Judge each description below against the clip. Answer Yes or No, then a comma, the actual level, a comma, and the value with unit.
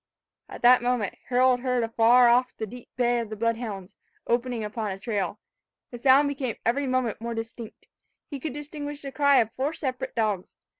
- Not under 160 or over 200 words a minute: Yes, average, 190 wpm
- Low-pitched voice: No, high, 245 Hz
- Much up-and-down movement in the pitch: No, narrow, 2.4 semitones